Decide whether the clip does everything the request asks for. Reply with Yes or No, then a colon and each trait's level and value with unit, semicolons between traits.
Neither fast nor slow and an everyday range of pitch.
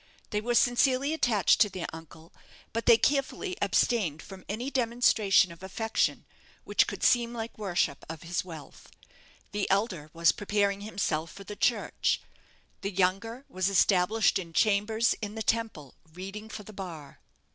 Yes: average, 155 wpm; average, 4.1 semitones